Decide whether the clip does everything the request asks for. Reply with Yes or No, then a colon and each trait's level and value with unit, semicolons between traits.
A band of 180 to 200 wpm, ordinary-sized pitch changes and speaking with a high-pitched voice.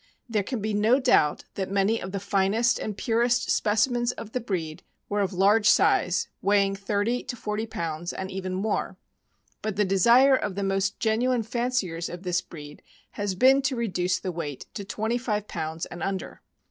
Yes: average, 185 wpm; average, 3.5 semitones; high, 205 Hz